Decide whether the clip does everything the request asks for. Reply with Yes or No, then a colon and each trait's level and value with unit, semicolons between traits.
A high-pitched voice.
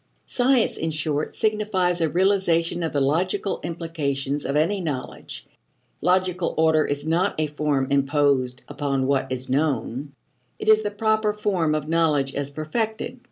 No: medium, 160 Hz